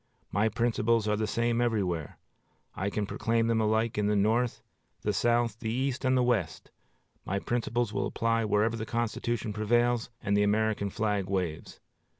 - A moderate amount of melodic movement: No, narrow, 2.3 semitones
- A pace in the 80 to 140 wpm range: No, average, 165 wpm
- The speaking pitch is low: Yes, low, 110 Hz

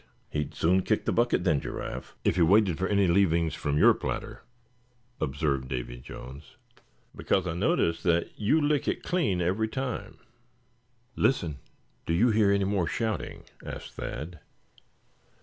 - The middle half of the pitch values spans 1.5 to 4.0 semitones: No, average, 5.1 semitones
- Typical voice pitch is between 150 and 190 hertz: No, very low, 90 Hz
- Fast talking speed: No, average, 150 wpm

